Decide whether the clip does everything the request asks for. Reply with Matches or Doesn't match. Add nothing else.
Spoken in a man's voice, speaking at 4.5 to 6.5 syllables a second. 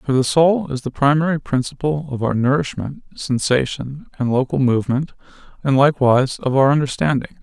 Matches